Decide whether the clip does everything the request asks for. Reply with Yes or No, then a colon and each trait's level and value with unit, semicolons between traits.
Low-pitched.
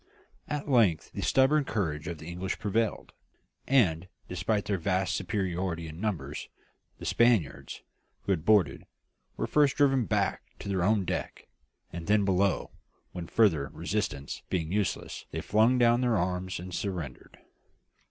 Yes: very low, 95 Hz